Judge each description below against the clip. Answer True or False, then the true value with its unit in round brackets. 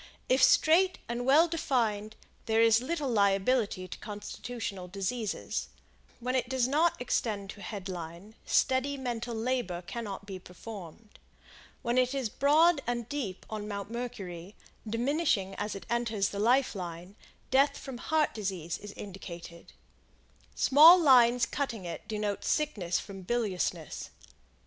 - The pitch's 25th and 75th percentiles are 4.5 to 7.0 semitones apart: True (4.8 semitones)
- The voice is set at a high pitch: True (225 Hz)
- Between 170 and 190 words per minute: False (135 wpm)